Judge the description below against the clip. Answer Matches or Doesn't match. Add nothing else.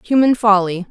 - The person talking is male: Doesn't match